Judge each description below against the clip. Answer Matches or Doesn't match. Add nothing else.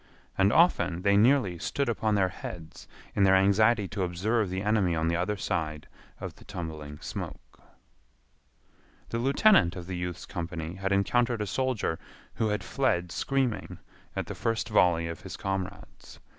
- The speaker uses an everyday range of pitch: Matches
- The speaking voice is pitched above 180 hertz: Doesn't match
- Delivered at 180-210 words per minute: Doesn't match